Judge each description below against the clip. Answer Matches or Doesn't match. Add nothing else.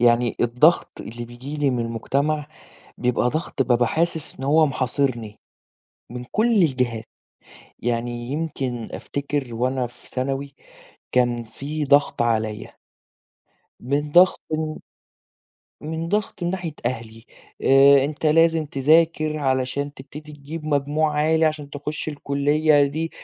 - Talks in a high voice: Doesn't match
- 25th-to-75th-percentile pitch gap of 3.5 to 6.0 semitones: Matches